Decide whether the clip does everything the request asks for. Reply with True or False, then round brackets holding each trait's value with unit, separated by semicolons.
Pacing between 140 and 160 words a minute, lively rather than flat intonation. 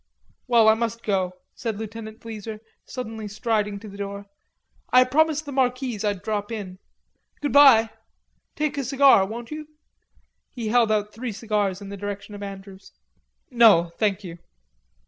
False (155 wpm; 3.2 semitones)